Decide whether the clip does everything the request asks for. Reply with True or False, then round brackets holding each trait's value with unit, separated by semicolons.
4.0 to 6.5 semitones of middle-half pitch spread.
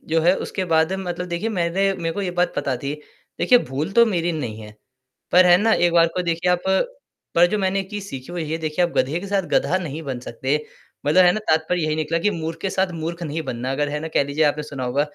False (3.4 semitones)